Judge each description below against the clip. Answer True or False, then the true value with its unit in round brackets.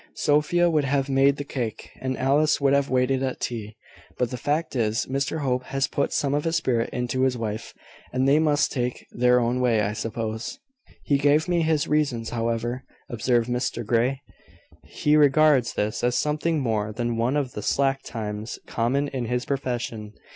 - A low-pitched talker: True (130 Hz)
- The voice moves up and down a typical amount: True (3.4 semitones)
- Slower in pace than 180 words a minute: False (185 wpm)